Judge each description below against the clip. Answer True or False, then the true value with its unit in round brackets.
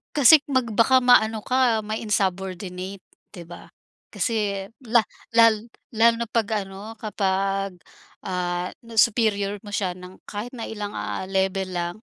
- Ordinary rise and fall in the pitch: True (3.1 semitones)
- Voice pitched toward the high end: True (205 Hz)